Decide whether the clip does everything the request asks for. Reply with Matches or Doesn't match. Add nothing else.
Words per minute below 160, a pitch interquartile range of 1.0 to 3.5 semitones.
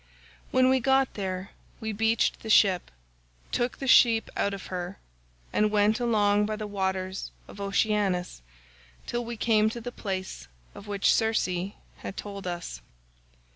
Matches